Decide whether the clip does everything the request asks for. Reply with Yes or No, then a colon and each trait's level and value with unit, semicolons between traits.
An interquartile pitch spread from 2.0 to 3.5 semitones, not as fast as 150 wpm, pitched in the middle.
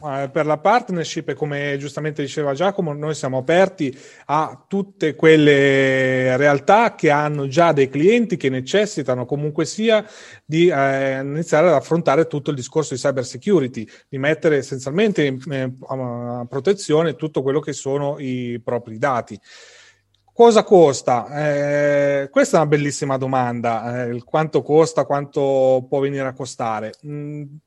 Yes: average, 2.9 semitones; average, 135 wpm; medium, 145 Hz